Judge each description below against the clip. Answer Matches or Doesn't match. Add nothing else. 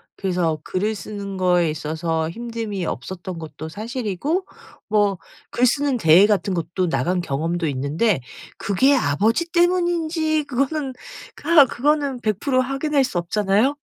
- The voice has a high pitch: Matches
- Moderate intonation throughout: Doesn't match